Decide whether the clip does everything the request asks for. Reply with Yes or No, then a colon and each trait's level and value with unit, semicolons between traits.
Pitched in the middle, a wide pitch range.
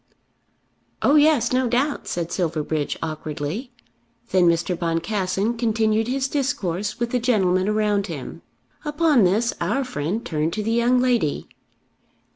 No: high, 215 Hz; wide, 6.3 semitones